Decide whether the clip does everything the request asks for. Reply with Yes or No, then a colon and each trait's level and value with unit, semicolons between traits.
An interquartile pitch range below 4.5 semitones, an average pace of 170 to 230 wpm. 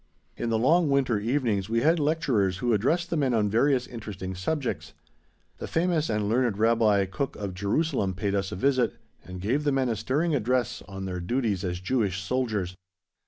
No: wide, 5.5 semitones; average, 185 wpm